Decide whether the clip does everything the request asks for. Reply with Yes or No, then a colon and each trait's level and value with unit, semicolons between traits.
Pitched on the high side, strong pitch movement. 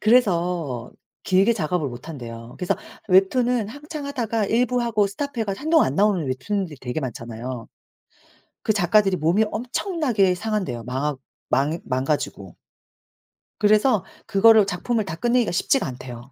Yes: high, 195 Hz; wide, 8.2 semitones